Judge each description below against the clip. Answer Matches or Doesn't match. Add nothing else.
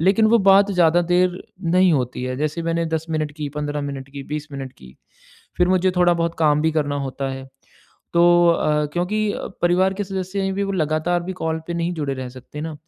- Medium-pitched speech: Matches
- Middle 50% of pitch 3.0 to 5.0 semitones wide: Matches